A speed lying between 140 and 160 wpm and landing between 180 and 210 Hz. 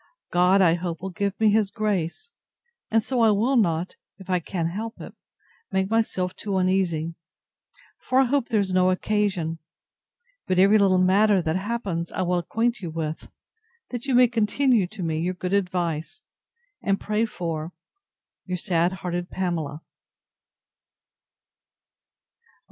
Yes: average, 150 wpm; high, 190 Hz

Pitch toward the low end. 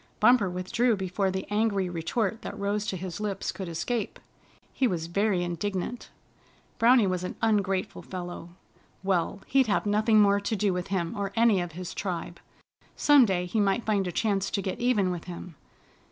No: high, 195 Hz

